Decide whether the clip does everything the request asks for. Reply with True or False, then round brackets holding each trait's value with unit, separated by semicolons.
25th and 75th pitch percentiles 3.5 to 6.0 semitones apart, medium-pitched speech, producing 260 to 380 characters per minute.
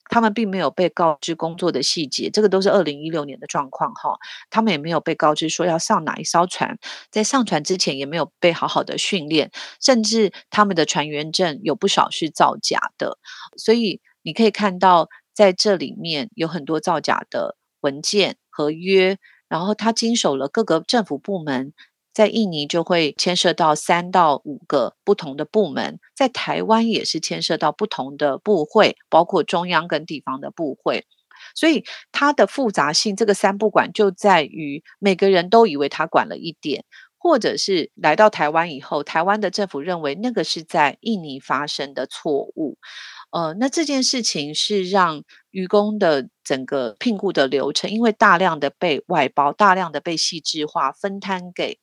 True (5.4 semitones; 180 Hz; 270 characters per minute)